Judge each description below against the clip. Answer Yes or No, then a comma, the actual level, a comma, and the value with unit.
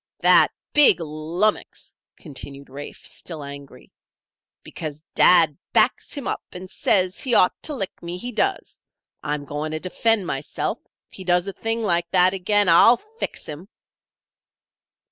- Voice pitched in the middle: Yes, medium, 180 Hz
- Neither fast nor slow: Yes, average, 150 wpm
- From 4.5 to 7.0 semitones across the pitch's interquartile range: Yes, average, 5.2 semitones